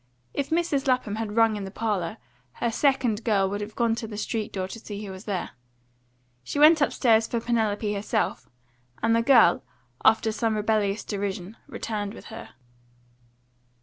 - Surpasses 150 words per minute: Yes, average, 170 wpm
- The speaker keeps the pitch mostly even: Yes, narrow, 2.1 semitones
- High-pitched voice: Yes, high, 220 Hz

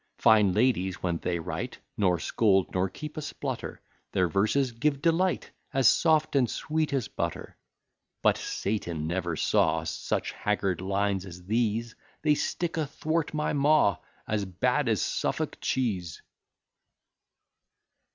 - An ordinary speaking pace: No, slow, 130 wpm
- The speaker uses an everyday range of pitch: No, wide, 7.8 semitones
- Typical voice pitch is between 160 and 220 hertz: No, low, 110 Hz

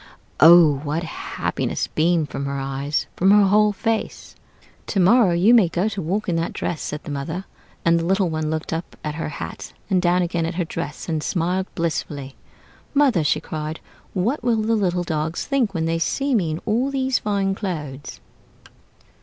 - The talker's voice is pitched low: No, medium, 175 Hz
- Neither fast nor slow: Yes, average, 185 wpm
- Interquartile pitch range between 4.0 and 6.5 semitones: Yes, average, 4.3 semitones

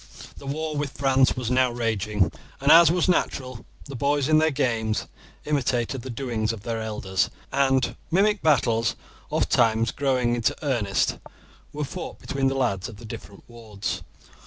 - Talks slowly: No, average, 160 wpm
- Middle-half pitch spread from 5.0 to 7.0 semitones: No, average, 3.9 semitones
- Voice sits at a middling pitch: No, low, 125 Hz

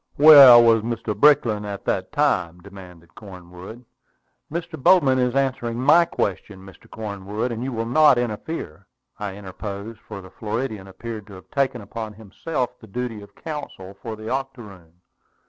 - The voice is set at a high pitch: No, low, 110 Hz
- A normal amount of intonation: Yes, average, 4.7 semitones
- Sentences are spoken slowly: No, average, 155 wpm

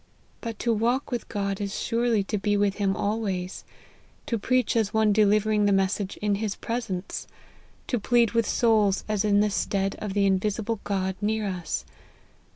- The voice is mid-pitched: No, high, 210 Hz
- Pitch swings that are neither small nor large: No, narrow, 2.2 semitones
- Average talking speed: Yes, average, 170 wpm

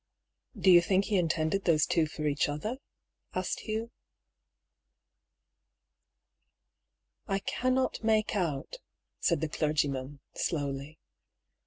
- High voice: No, medium, 165 Hz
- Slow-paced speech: Yes, slow, 115 wpm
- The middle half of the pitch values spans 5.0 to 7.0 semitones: Yes, wide, 5.4 semitones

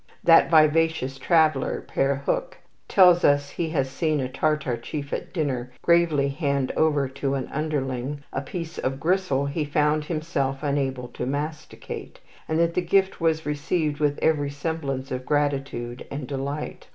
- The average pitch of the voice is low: No, medium, 145 Hz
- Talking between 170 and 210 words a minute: No, average, 155 wpm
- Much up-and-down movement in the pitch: No, average, 2.8 semitones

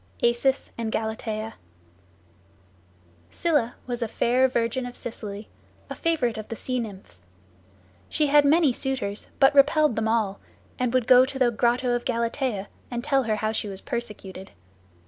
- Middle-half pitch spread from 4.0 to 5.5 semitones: No, average, 3.1 semitones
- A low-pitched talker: No, high, 240 Hz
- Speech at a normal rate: Yes, average, 155 wpm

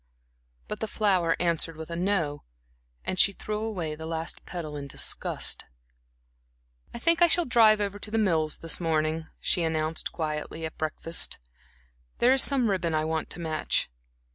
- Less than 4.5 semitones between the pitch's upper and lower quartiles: No, average, 4.8 semitones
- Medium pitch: Yes, medium, 170 Hz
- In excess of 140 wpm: Yes, average, 175 wpm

